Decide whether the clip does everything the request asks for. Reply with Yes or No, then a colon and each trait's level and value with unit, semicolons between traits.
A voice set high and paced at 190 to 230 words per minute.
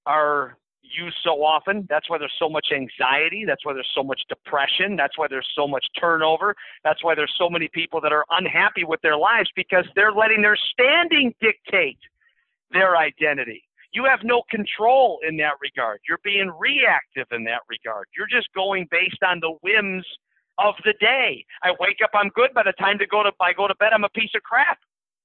Yes: high, 195 Hz; average, 200 wpm